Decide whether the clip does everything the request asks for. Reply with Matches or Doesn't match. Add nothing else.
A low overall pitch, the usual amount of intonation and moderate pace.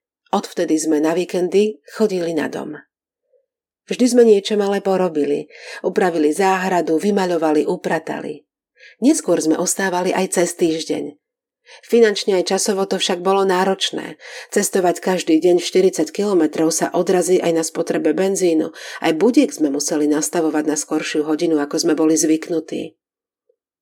Doesn't match